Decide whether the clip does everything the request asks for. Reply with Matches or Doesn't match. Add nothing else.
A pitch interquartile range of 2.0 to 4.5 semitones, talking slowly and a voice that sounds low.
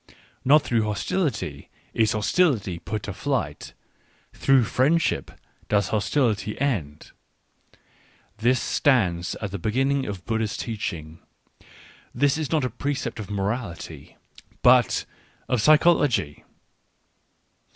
Doesn't match